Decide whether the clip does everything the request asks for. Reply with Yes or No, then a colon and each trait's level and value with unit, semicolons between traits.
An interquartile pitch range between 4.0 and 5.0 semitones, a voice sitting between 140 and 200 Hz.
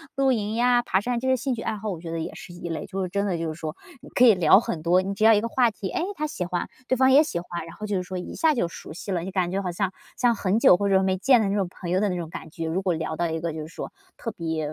Yes: average, 4.6 semitones; high, 190 Hz